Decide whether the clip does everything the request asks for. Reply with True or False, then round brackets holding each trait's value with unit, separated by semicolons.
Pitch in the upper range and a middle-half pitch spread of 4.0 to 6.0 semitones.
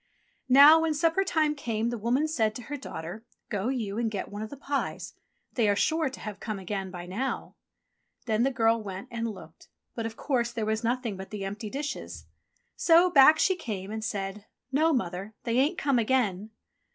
True (230 Hz; 5.0 semitones)